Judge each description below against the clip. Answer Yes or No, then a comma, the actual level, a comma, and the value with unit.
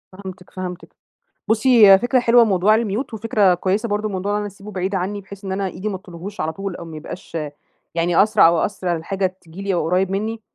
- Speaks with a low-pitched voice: No, high, 195 Hz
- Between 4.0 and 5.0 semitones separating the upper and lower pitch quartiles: No, narrow, 2.5 semitones